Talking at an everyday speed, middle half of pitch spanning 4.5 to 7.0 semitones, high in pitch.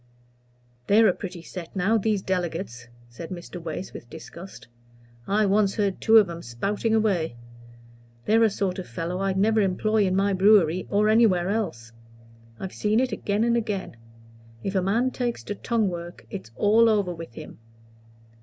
No: average, 170 wpm; average, 3.5 semitones; high, 195 Hz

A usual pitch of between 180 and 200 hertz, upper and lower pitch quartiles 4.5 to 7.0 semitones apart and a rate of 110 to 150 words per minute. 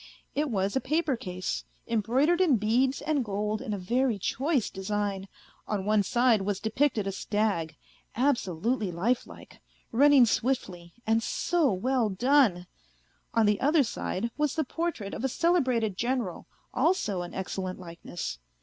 No: high, 225 Hz; average, 5.3 semitones; average, 145 wpm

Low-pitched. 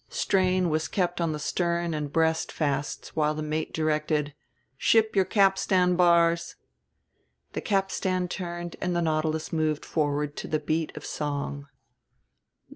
No: medium, 160 Hz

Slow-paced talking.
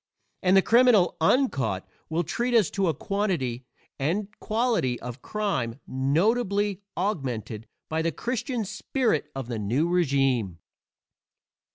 Yes: slow, 125 wpm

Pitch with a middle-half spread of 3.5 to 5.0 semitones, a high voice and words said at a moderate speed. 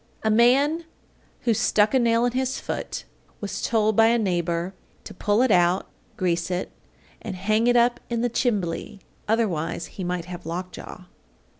Yes: average, 4.7 semitones; high, 215 Hz; average, 165 wpm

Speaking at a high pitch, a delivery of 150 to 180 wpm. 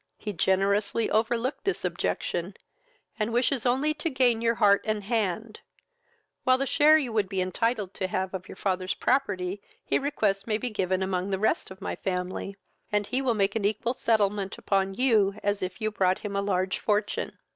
No: high, 210 Hz; average, 190 wpm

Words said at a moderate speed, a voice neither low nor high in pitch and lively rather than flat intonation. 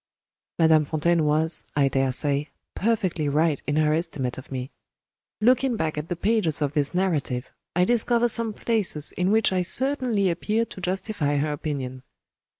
Yes: average, 155 wpm; medium, 165 Hz; wide, 6.2 semitones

